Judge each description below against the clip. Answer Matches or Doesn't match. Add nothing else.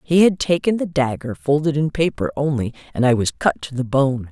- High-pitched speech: Doesn't match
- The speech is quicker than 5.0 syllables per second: Matches